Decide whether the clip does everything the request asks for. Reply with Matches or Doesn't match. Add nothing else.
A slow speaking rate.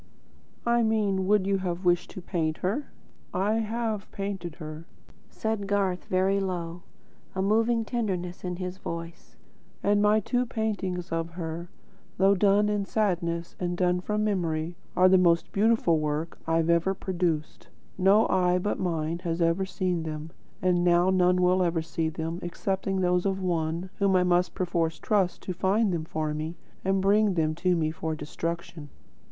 Doesn't match